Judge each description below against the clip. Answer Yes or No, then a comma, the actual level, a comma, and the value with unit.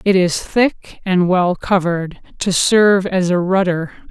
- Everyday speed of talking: Yes, average, 160 wpm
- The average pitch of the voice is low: No, medium, 185 Hz